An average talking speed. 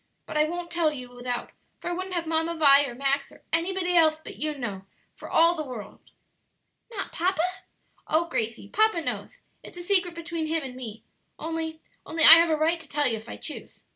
No: fast, 210 wpm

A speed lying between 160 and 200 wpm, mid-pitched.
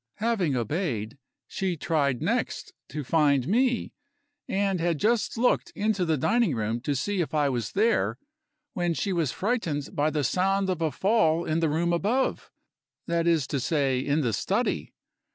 Yes: average, 170 wpm; medium, 165 Hz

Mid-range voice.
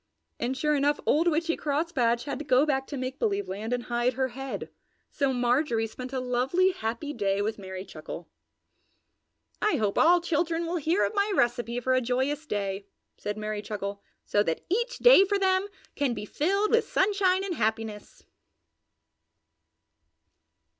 No: very high, 265 Hz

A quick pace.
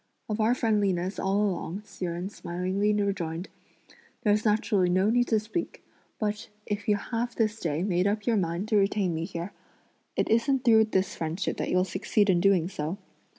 No: average, 180 wpm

